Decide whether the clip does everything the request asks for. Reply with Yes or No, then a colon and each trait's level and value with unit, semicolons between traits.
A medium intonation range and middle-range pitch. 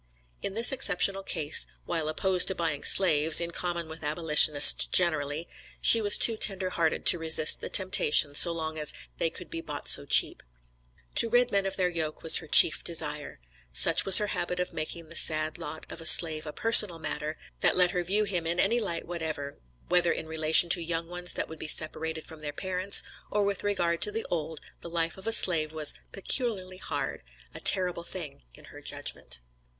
Yes: average, 3.1 semitones; medium, 170 Hz